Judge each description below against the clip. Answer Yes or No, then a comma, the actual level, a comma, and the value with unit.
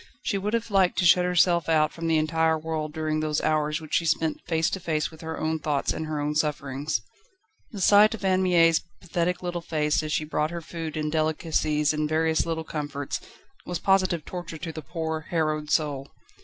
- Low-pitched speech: No, medium, 160 Hz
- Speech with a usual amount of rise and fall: No, narrow, 2.0 semitones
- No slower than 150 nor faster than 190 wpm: No, fast, 205 wpm